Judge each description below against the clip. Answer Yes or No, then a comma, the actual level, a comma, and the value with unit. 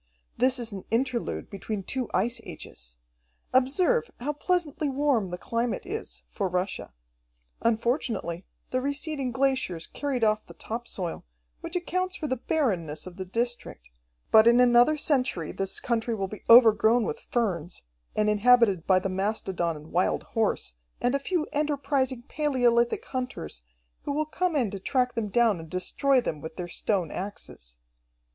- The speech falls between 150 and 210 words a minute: Yes, average, 155 wpm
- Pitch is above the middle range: Yes, high, 235 Hz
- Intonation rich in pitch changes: Yes, wide, 5.9 semitones